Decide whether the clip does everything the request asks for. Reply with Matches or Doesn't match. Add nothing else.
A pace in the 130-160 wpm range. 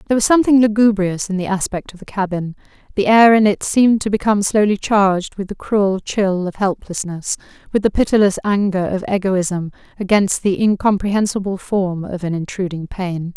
Doesn't match